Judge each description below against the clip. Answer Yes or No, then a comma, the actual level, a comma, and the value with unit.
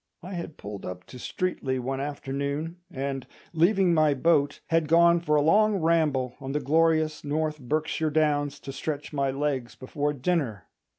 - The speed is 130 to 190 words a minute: Yes, average, 165 wpm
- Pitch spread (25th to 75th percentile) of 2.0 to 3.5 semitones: Yes, average, 3.1 semitones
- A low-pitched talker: No, medium, 150 Hz